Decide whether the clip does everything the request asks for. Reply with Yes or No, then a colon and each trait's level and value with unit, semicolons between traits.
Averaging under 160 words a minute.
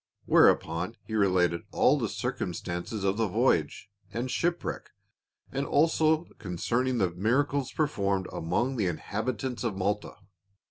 Yes: slow, 135 wpm